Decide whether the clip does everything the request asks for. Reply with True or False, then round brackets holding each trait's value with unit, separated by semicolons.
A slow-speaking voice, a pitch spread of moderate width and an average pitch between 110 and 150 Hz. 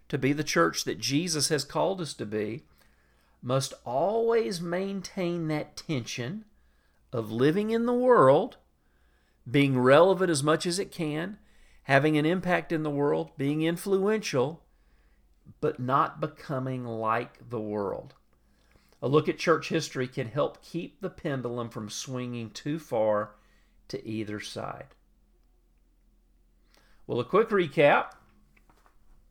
False (130 wpm; 7.9 semitones; 135 Hz)